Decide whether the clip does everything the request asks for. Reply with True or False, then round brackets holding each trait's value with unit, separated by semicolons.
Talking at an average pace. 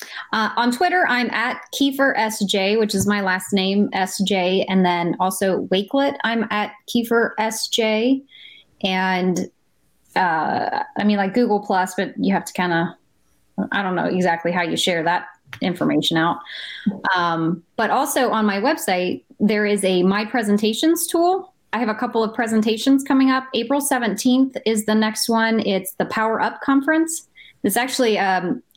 True (165 wpm)